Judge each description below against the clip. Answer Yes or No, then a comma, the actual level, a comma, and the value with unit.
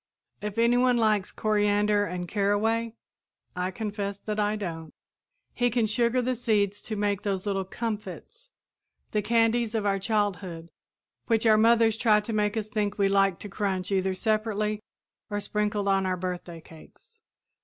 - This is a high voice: Yes, high, 210 Hz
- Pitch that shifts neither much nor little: No, narrow, 2.1 semitones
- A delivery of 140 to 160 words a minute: Yes, average, 155 wpm